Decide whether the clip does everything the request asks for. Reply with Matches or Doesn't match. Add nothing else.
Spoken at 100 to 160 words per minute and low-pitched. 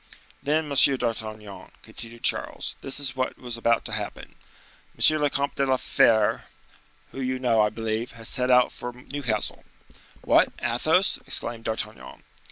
Matches